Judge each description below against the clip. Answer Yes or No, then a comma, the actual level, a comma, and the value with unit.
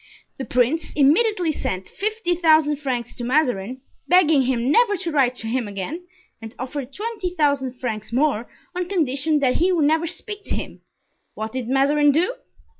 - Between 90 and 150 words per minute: No, average, 170 wpm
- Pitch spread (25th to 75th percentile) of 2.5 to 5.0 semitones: No, wide, 5.6 semitones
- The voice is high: Yes, very high, 290 Hz